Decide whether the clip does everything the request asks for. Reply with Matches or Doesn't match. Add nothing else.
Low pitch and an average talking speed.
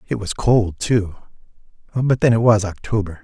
Matches